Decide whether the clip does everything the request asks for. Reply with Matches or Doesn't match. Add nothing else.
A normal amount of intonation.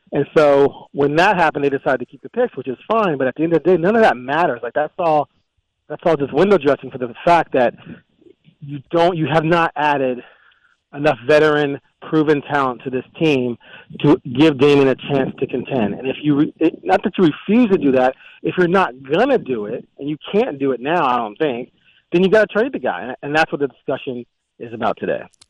Matches